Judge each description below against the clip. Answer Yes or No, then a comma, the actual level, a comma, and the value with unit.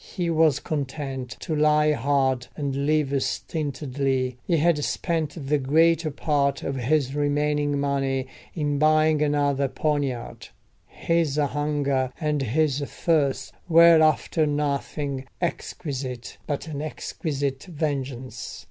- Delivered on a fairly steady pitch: Yes, narrow, 2.2 semitones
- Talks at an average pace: No, slow, 110 wpm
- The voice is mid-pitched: Yes, medium, 145 Hz